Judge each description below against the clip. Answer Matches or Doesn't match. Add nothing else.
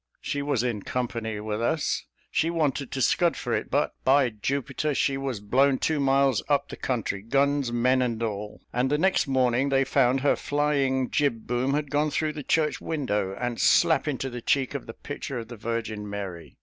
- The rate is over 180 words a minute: Matches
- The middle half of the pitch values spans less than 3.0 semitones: Doesn't match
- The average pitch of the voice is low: Matches